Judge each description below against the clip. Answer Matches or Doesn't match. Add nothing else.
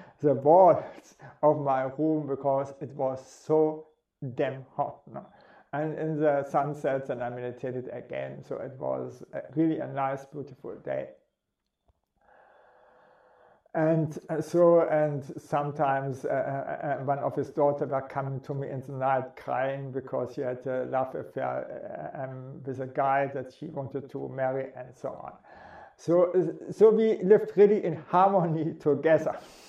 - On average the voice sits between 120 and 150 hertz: Matches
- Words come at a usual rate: Matches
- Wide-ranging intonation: Doesn't match